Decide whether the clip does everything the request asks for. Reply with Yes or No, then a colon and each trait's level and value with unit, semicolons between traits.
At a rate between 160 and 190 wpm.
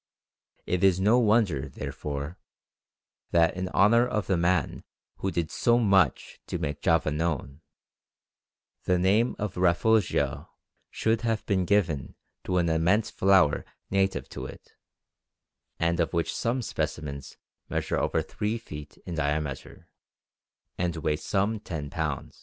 No: slow, 135 wpm